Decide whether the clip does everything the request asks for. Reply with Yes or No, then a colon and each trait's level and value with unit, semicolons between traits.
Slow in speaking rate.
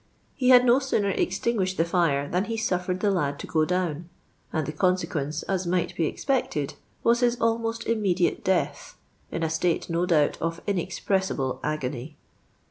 No: average, 165 wpm